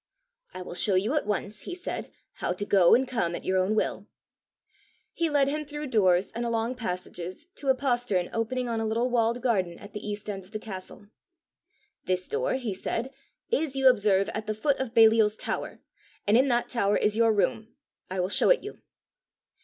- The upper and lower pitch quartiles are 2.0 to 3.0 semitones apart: No, average, 4.3 semitones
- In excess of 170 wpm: Yes, average, 200 wpm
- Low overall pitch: No, high, 225 Hz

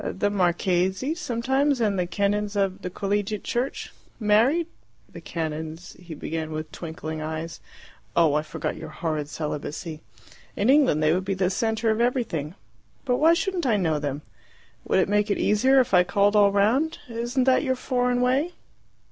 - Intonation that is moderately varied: No, wide, 7.1 semitones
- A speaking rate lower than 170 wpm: No, average, 175 wpm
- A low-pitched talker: No, high, 200 Hz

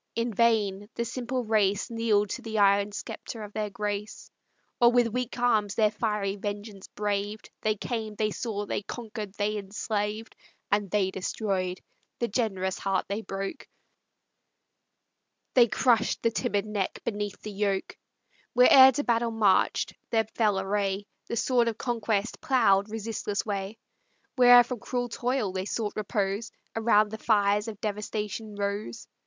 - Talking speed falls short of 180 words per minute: Yes, average, 150 wpm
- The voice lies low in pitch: No, high, 210 Hz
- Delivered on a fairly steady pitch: Yes, narrow, 2.3 semitones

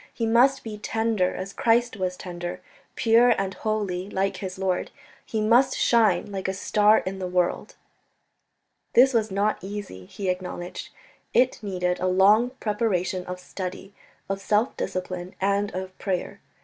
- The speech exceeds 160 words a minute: No, average, 150 wpm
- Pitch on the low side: No, high, 195 Hz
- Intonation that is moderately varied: Yes, average, 3.1 semitones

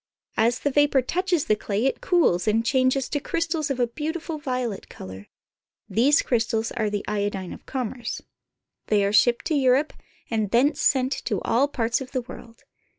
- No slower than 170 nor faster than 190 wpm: Yes, average, 175 wpm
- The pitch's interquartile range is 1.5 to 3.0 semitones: No, average, 4.5 semitones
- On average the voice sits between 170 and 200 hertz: No, very high, 250 Hz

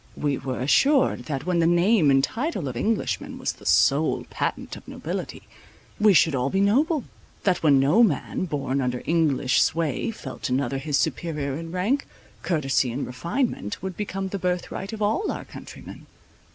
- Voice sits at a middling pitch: Yes, medium, 165 Hz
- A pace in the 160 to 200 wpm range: Yes, average, 175 wpm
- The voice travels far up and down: Yes, wide, 6.6 semitones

